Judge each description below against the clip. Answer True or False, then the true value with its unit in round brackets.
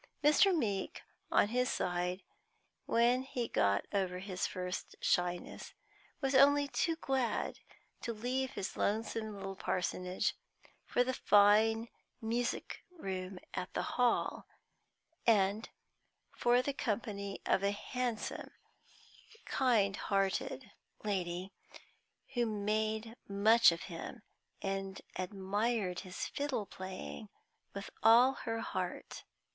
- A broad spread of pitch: False (4.1 semitones)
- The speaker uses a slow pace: True (110 wpm)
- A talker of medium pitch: False (215 Hz)